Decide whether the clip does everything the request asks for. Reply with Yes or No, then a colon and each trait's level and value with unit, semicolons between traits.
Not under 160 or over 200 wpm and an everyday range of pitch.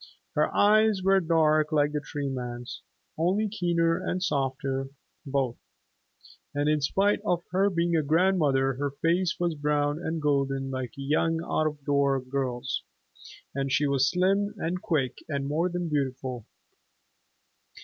No: average, 150 wpm; average, 4.0 semitones